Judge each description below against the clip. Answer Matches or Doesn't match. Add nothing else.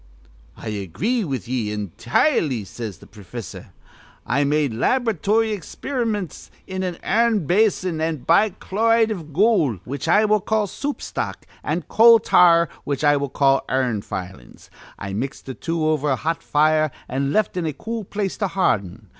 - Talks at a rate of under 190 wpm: Matches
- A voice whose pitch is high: Doesn't match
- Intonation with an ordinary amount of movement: Doesn't match